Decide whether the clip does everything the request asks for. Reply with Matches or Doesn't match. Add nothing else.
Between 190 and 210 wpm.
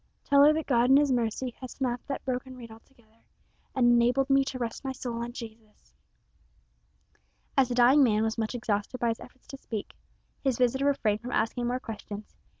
Matches